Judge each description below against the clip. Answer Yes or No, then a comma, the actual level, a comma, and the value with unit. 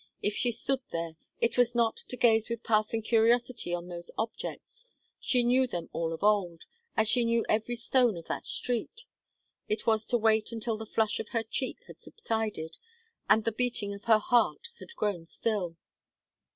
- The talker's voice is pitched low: No, high, 225 Hz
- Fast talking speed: No, average, 180 wpm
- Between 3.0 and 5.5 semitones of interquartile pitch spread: No, narrow, 2.6 semitones